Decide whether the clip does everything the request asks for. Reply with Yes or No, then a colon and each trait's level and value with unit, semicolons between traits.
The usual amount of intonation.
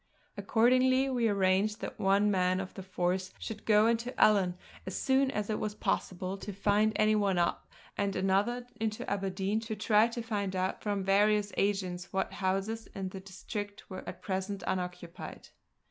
No: narrow, 2.3 semitones